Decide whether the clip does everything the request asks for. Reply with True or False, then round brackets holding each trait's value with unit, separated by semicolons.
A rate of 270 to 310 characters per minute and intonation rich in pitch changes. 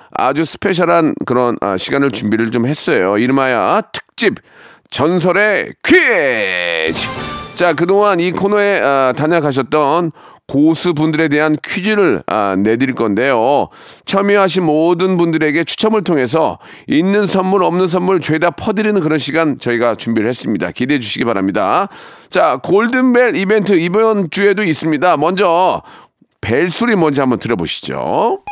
True (300 characters per minute; 6.3 semitones)